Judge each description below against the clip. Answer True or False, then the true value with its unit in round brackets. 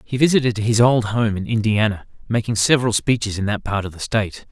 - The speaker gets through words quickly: True (215 wpm)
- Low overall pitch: True (110 Hz)